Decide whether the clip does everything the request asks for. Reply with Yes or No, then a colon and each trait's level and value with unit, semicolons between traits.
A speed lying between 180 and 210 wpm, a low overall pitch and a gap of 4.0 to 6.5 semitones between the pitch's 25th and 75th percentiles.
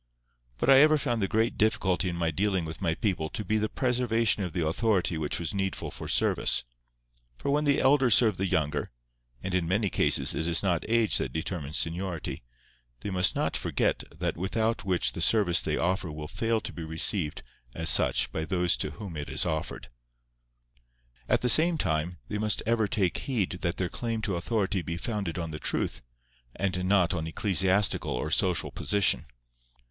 Yes: average, 185 wpm; very low, 95 Hz; average, 4.8 semitones